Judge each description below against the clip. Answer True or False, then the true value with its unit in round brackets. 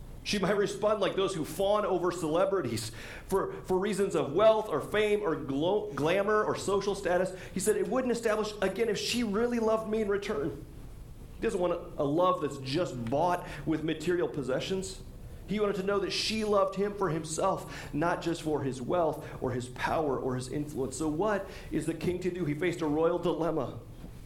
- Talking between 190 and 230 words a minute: True (200 wpm)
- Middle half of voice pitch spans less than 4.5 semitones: False (4.9 semitones)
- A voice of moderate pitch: True (180 Hz)